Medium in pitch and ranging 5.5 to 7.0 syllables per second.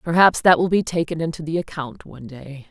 Yes: medium, 160 Hz; 5.8 syllables/s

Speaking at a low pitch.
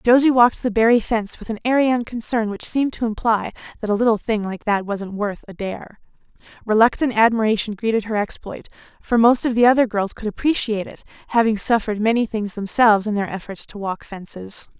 No: high, 220 Hz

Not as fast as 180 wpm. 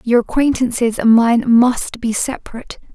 Yes: average, 140 wpm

